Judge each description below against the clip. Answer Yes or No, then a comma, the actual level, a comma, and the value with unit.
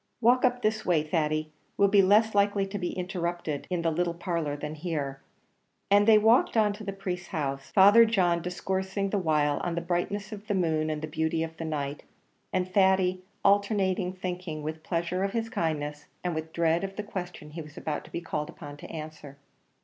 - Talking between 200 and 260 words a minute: Yes, fast, 205 wpm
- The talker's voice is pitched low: No, medium, 175 Hz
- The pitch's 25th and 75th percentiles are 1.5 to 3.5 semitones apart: No, average, 4.1 semitones